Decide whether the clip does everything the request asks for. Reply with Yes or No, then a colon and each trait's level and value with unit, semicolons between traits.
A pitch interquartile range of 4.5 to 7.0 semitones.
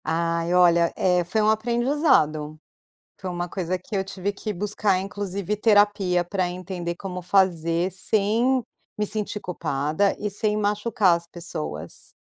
No: average, 3.2 semitones